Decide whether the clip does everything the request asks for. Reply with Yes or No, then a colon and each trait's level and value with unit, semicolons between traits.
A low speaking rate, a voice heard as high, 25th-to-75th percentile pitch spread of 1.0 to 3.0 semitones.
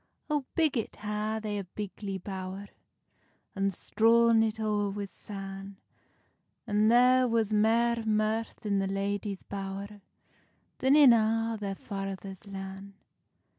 Yes: slow, 125 wpm; high, 210 Hz; narrow, 2.4 semitones